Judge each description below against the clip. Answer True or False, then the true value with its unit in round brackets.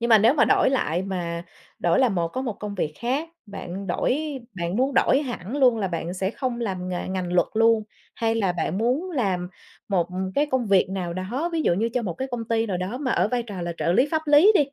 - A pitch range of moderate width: False (5.7 semitones)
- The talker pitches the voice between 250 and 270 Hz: False (215 Hz)